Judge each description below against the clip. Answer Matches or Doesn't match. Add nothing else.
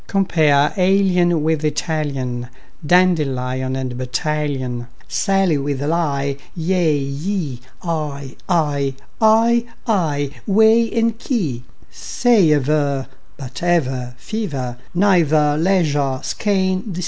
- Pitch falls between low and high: Matches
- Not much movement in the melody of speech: Doesn't match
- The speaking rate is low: Matches